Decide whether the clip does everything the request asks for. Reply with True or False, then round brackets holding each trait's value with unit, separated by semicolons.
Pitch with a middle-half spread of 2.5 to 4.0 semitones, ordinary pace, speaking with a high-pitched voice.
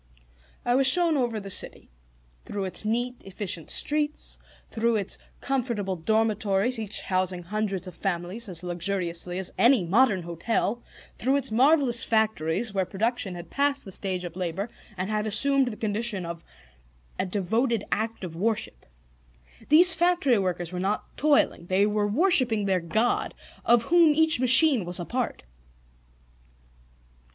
False (5.0 semitones; 145 wpm; 215 Hz)